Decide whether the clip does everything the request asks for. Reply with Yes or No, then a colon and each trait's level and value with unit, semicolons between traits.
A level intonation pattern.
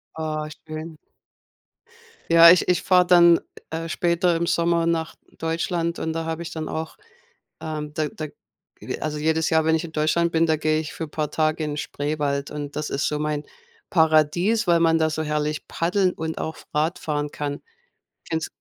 Yes: narrow, 1.7 semitones